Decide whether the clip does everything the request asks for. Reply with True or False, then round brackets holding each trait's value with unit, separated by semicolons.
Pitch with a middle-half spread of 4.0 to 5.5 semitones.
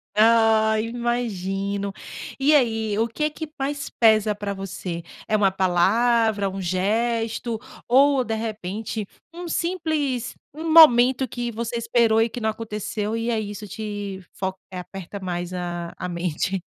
False (3.4 semitones)